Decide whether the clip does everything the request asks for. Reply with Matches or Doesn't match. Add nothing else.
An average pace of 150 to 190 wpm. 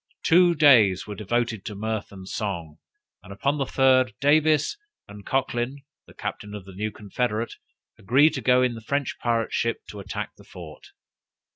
Matches